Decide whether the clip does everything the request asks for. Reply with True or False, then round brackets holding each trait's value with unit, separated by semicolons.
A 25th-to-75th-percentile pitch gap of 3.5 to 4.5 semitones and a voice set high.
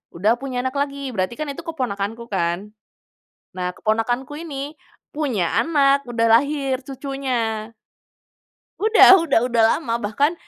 True (4.1 semitones; 260 Hz)